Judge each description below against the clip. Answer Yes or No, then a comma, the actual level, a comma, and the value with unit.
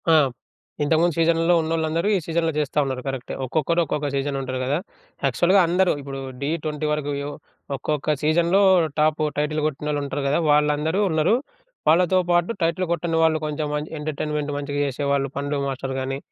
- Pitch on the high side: No, medium, 150 Hz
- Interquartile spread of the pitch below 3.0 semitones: Yes, narrow, 2.5 semitones